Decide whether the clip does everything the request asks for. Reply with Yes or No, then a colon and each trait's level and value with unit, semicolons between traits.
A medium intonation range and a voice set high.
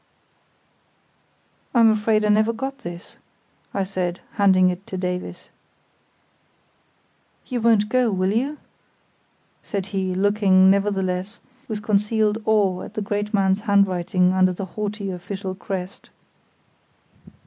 No: narrow, 2.2 semitones; high, 200 Hz